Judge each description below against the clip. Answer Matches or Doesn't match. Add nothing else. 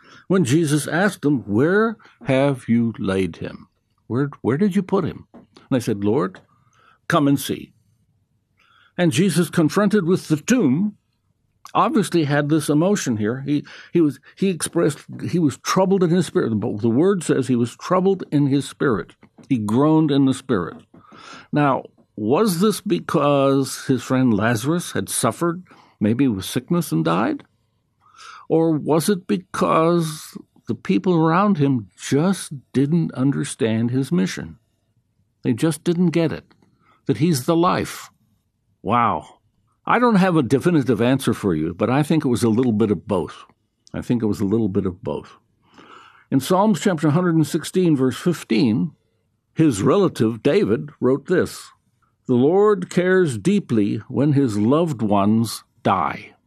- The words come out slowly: Doesn't match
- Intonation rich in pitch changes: Matches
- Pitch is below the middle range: Doesn't match